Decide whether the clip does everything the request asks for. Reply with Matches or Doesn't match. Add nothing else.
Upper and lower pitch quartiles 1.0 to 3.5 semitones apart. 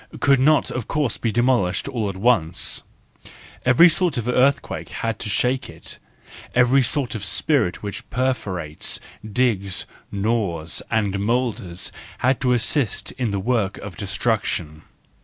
Doesn't match